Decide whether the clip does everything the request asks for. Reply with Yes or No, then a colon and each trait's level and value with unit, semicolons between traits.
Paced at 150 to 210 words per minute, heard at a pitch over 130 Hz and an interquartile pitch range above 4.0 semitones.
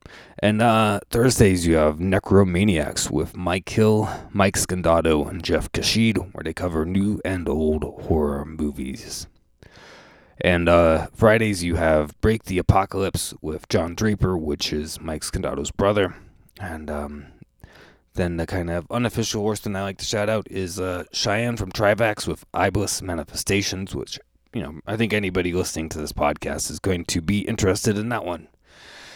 No: average, 160 wpm; very low, 90 Hz; average, 4.4 semitones